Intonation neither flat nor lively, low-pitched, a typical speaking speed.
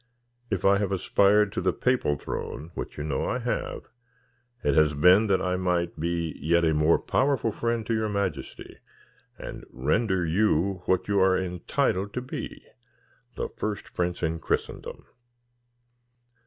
Yes: average, 3.7 semitones; very low, 95 Hz; average, 155 wpm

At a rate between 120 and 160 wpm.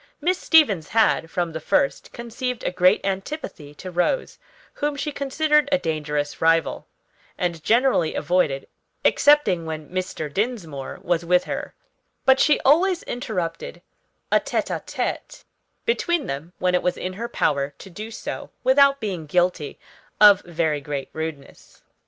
Yes: average, 145 wpm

